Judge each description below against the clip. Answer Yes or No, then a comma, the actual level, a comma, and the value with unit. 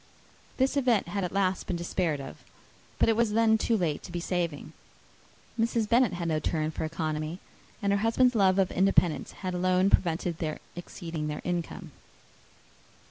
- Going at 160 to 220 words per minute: Yes, average, 170 wpm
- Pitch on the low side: No, medium, 180 Hz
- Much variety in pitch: No, average, 4.1 semitones